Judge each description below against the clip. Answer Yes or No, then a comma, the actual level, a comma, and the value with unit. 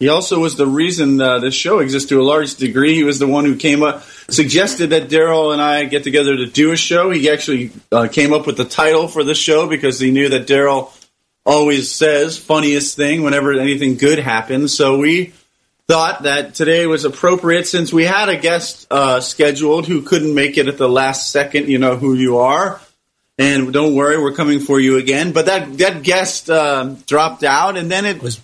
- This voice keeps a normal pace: No, fast, 215 wpm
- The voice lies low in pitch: No, medium, 145 Hz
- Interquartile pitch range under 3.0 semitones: Yes, narrow, 2.6 semitones